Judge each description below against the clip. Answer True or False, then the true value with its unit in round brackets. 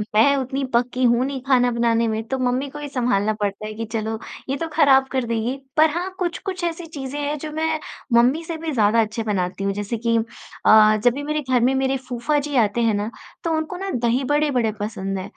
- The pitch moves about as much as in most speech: True (4.6 semitones)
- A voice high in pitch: True (250 Hz)